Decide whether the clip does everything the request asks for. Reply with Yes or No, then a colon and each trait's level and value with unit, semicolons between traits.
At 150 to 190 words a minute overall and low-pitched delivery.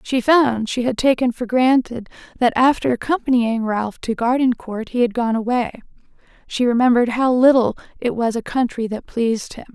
No: average, 170 wpm; high, 240 Hz